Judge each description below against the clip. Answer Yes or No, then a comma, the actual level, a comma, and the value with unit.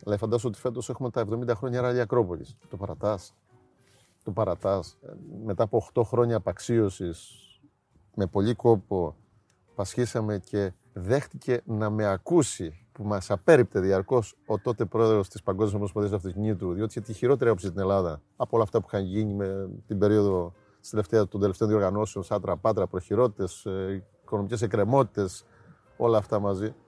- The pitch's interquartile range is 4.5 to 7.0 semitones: No, average, 3.0 semitones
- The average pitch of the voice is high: No, low, 105 Hz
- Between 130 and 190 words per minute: Yes, average, 150 wpm